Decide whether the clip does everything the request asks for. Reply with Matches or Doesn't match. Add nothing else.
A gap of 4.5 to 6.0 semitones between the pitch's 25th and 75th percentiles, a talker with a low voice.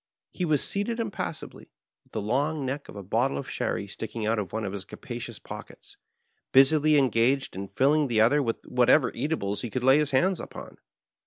Matches